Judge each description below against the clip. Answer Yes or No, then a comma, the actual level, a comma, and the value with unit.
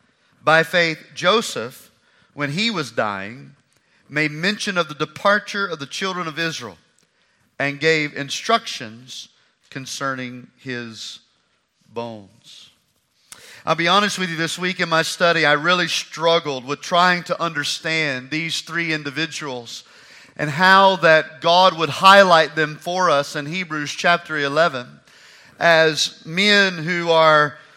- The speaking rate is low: Yes, slow, 130 wpm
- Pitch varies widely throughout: No, average, 3.5 semitones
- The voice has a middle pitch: Yes, medium, 160 Hz